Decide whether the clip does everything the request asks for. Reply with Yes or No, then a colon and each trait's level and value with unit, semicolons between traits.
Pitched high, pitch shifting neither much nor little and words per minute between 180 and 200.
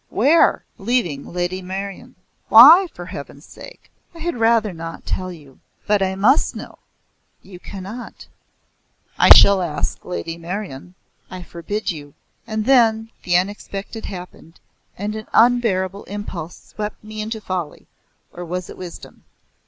No: high, 195 Hz; average, 3.7 semitones; slow, 135 wpm